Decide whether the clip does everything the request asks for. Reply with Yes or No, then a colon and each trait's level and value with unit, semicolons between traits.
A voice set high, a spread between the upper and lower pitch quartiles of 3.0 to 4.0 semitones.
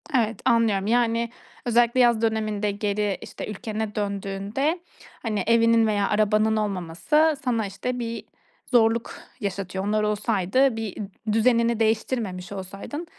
No: high, 220 Hz; narrow, 2.4 semitones